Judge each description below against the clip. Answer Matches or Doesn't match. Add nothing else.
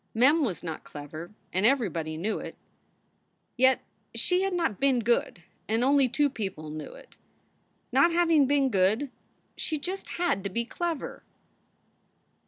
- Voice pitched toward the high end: Matches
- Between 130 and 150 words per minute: Matches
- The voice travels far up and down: Matches